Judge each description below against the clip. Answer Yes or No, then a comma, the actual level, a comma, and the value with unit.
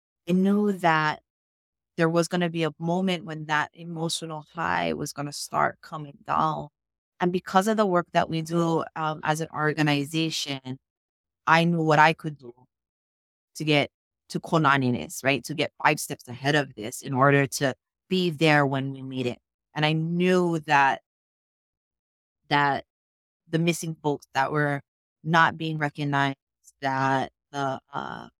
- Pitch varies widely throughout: No, average, 3.5 semitones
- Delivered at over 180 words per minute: No, average, 160 wpm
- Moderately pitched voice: Yes, medium, 150 Hz